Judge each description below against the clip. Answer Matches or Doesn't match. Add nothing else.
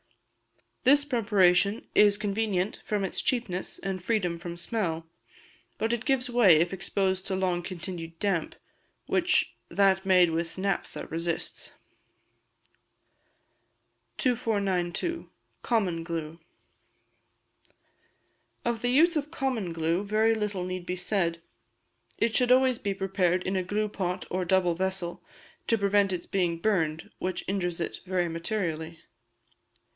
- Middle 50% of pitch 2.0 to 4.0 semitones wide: Matches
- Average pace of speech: Doesn't match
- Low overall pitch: Doesn't match